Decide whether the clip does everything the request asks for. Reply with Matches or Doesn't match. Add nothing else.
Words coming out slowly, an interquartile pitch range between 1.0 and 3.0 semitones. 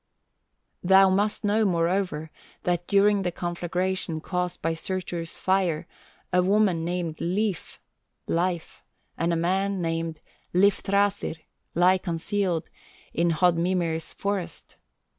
Matches